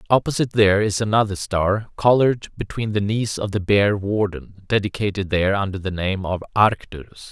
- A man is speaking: Yes, male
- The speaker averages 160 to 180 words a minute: Yes, average, 165 wpm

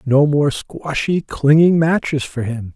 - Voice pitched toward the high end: No, medium, 145 Hz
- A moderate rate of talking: Yes, average, 150 wpm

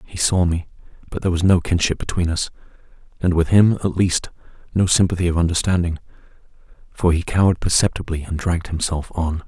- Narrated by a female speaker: No, male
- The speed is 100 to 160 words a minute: No, average, 170 wpm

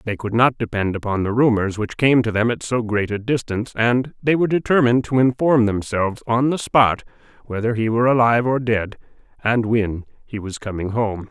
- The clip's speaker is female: No, male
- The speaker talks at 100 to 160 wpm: No, average, 200 wpm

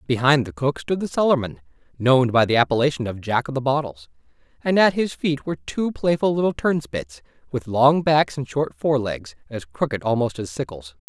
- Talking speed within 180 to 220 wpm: Yes, average, 190 wpm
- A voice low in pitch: Yes, low, 125 Hz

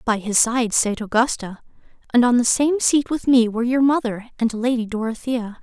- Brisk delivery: No, average, 190 wpm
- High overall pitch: Yes, high, 240 Hz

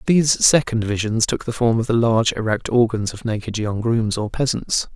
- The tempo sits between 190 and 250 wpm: Yes, fast, 205 wpm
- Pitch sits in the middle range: No, low, 115 Hz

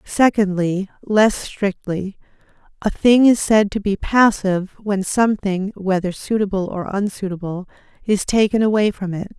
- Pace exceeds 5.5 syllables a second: No, 4.5 syllables/s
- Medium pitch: No, high, 200 Hz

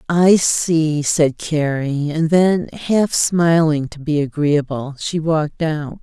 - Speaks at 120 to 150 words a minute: Yes, average, 140 wpm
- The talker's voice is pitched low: No, medium, 155 Hz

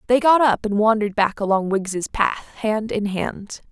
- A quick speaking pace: No, average, 195 wpm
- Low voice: No, high, 215 Hz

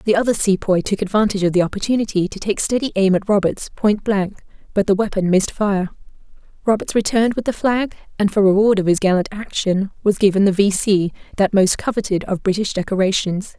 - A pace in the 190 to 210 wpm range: Yes, average, 195 wpm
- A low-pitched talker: No, high, 200 Hz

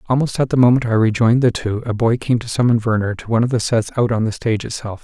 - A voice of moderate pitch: No, low, 115 Hz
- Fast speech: Yes, fast, 285 wpm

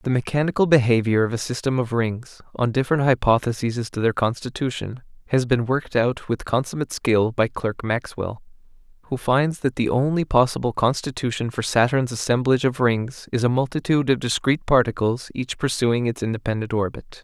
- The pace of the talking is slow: No, average, 165 wpm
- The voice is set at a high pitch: No, low, 125 Hz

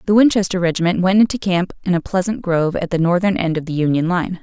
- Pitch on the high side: No, medium, 180 Hz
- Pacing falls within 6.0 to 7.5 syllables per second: Yes, 6.5 syllables/s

